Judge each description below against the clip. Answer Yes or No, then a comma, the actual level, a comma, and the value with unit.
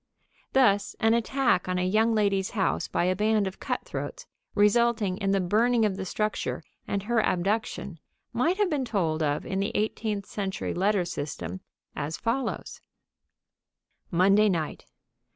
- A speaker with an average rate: Yes, average, 150 wpm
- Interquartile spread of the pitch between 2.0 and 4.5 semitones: Yes, average, 3.4 semitones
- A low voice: No, high, 205 Hz